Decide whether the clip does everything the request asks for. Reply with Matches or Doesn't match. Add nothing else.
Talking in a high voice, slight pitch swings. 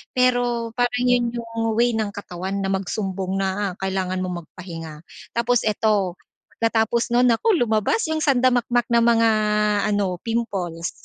Doesn't match